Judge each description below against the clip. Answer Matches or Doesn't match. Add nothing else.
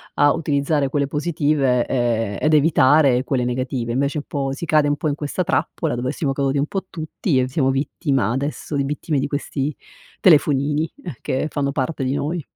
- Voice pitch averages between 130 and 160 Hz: Matches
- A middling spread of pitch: Doesn't match